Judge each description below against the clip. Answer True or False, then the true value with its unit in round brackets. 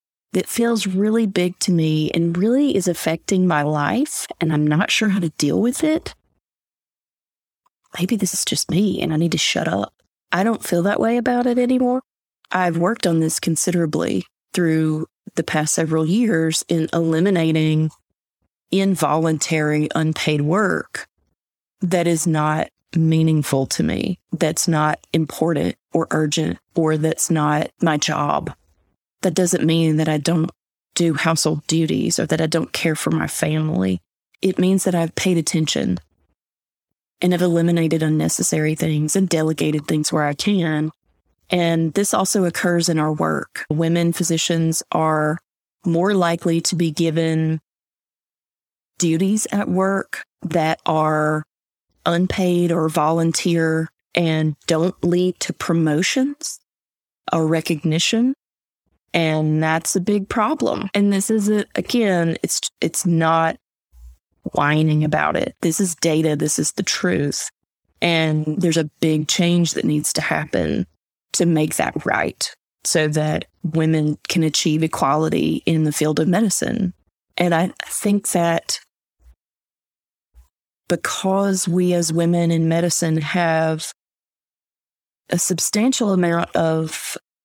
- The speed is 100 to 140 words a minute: True (135 wpm)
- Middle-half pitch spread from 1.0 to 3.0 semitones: True (2.7 semitones)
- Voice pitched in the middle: True (165 Hz)